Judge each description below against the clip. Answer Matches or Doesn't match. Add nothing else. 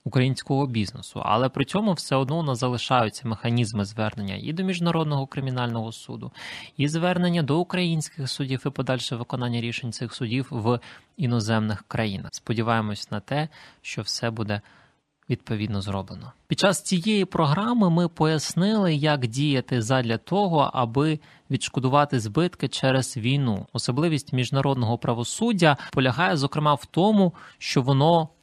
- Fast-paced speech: Doesn't match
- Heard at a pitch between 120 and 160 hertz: Matches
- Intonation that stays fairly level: Doesn't match